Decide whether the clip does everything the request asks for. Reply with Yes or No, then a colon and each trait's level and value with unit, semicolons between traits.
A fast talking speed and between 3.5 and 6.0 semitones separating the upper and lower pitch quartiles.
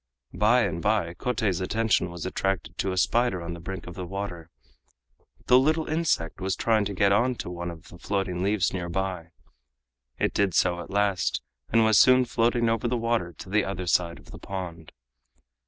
No: average, 195 wpm; average, 4.5 semitones